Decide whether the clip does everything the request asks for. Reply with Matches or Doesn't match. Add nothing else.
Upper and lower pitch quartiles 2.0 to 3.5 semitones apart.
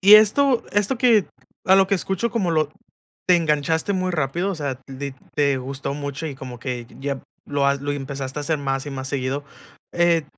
Doesn't match